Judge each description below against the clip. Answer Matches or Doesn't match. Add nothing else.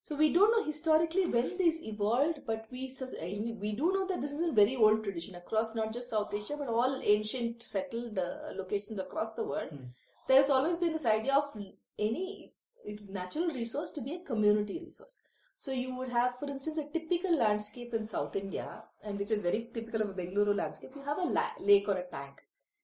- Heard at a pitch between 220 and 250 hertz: Matches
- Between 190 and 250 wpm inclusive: Matches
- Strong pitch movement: Matches